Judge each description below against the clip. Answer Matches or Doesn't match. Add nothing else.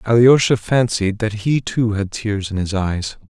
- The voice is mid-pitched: Doesn't match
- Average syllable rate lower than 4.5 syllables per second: Matches